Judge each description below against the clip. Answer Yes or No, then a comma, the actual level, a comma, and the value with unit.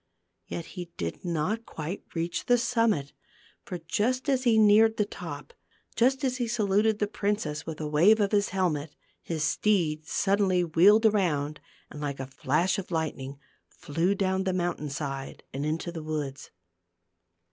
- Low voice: No, medium, 180 Hz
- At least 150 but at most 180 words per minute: Yes, average, 160 wpm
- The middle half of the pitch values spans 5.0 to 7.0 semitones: Yes, wide, 5.5 semitones